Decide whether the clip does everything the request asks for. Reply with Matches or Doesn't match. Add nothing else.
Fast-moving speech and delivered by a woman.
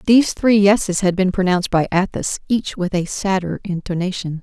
Doesn't match